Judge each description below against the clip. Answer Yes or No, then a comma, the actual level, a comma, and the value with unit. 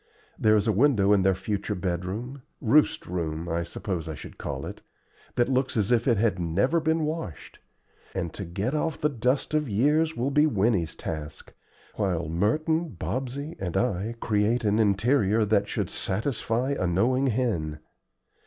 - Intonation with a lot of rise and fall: Yes, wide, 6.0 semitones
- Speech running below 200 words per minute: Yes, average, 165 wpm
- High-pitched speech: No, low, 110 Hz